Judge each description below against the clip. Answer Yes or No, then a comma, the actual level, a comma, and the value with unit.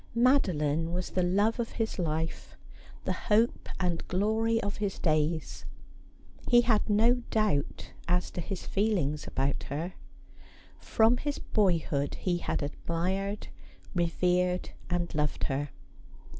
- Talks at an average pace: No, slow, 125 wpm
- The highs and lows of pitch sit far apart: No, average, 4.8 semitones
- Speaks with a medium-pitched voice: Yes, medium, 180 Hz